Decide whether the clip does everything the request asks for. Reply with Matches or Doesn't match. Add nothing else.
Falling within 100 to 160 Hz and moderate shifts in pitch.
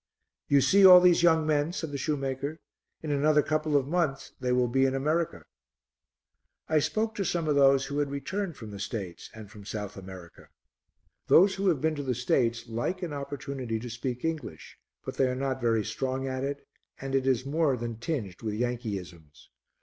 Matches